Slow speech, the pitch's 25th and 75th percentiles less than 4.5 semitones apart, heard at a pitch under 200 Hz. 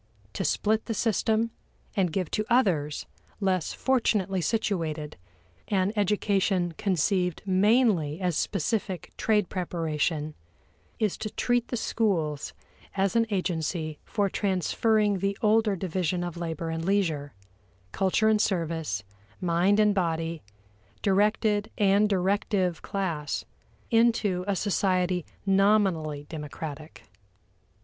Yes: slow, 110 wpm; average, 4.0 semitones; high, 190 Hz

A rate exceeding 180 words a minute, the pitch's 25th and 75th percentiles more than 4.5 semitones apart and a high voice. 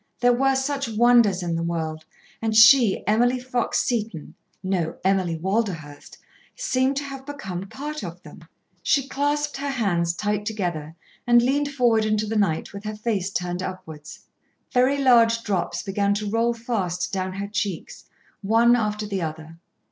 No: average, 160 wpm; average, 4.9 semitones; high, 215 Hz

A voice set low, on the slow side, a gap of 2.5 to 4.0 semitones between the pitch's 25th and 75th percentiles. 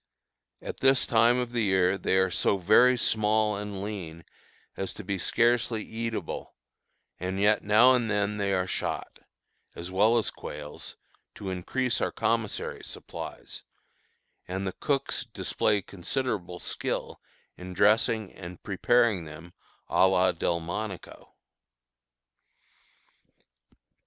Yes: low, 100 Hz; slow, 120 wpm; average, 3.6 semitones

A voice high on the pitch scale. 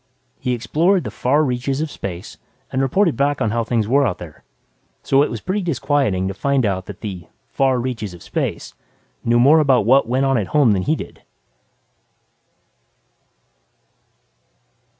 No: low, 130 Hz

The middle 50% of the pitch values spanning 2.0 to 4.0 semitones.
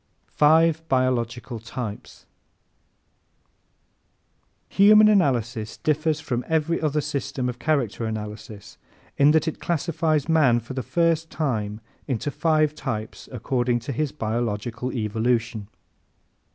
No: average, 5.2 semitones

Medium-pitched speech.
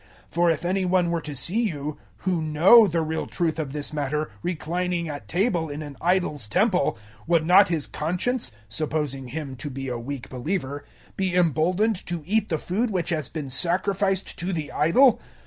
Yes: medium, 165 Hz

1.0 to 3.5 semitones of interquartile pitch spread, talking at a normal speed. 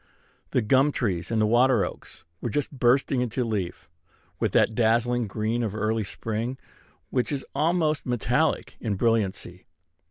Yes: average, 3.1 semitones; average, 145 wpm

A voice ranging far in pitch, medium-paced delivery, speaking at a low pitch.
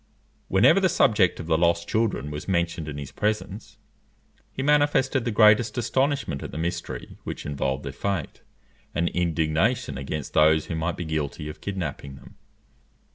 Yes: wide, 6.1 semitones; average, 160 wpm; very low, 85 Hz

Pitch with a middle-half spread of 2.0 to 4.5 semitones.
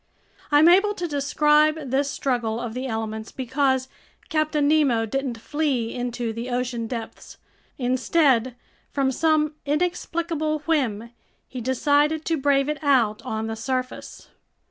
Yes: average, 4.0 semitones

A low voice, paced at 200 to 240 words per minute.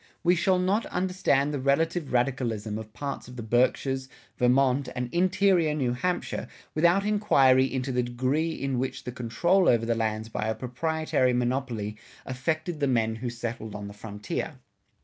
No: low, 130 Hz; average, 165 wpm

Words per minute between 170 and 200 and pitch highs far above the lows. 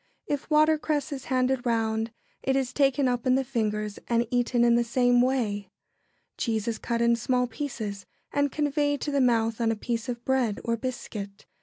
No: average, 185 wpm; average, 2.9 semitones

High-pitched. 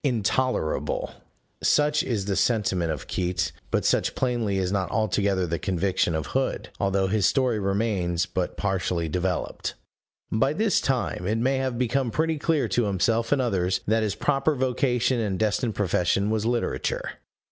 No: low, 110 Hz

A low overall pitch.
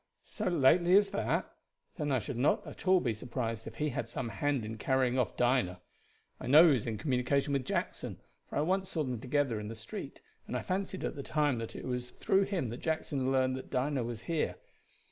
Yes: low, 130 Hz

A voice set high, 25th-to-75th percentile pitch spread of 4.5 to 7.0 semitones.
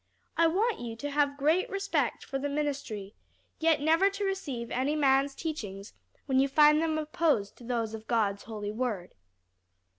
Yes: very high, 280 Hz; wide, 5.4 semitones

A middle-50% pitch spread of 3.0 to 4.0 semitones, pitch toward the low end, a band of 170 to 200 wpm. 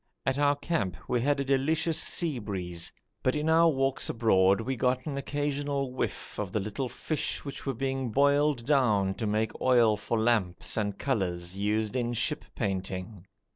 No: average, 5.2 semitones; low, 125 Hz; average, 175 wpm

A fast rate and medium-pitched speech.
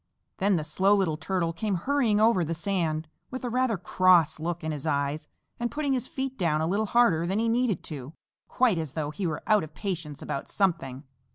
Yes: fast, 210 wpm; medium, 180 Hz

